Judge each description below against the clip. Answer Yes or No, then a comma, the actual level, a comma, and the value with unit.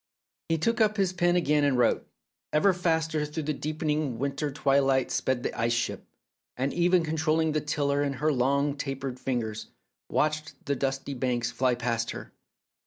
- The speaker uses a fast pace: No, average, 170 wpm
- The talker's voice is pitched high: No, medium, 145 Hz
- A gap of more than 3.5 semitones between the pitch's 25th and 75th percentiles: No, average, 3.2 semitones